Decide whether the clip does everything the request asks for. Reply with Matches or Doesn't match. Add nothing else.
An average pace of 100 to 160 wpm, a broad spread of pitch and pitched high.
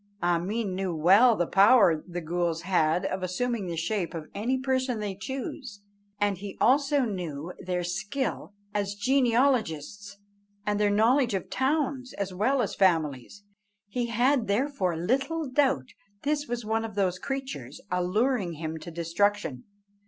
Matches